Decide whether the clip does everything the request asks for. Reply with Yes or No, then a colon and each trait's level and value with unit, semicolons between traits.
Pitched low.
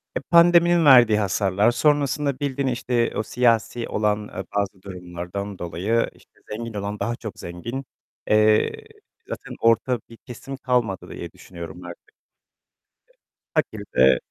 Yes: low, 110 Hz